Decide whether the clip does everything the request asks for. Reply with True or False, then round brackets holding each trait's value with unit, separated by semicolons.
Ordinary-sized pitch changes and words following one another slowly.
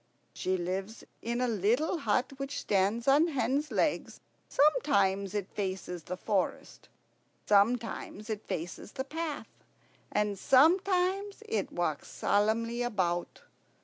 False (6.2 semitones; 115 wpm)